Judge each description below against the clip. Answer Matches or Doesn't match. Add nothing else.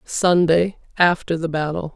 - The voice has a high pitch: Doesn't match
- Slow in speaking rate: Matches